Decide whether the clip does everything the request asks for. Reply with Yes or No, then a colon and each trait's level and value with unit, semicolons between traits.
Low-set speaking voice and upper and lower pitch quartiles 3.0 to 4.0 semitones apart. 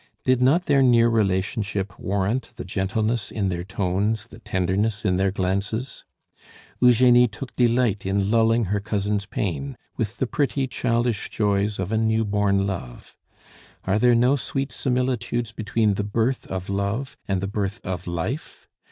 Yes: low, 105 Hz; average, 3.6 semitones